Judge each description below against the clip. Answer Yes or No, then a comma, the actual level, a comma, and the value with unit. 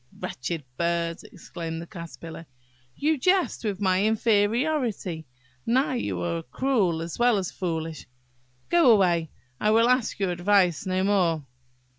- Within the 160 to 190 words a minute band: No, slow, 135 wpm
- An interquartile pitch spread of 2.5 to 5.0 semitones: No, wide, 5.6 semitones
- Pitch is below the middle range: No, medium, 185 Hz